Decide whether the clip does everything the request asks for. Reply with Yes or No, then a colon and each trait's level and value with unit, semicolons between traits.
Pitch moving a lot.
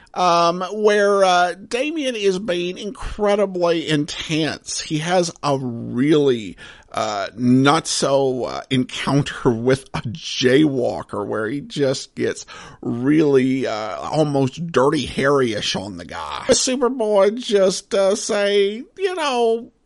Yes: wide, 6.7 semitones